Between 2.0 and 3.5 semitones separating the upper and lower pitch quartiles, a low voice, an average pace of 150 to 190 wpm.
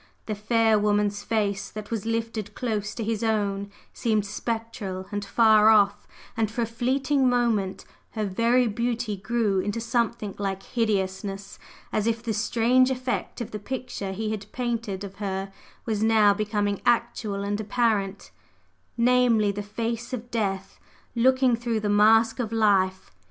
No: narrow, 2.4 semitones; high, 220 Hz; average, 155 wpm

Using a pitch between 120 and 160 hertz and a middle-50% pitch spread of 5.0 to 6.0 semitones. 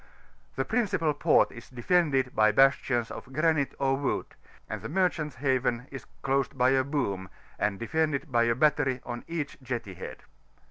No: low, 135 Hz; average, 3.8 semitones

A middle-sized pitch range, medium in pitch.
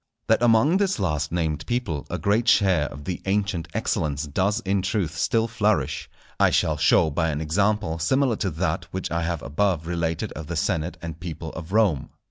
No: average, 4.9 semitones; very low, 90 Hz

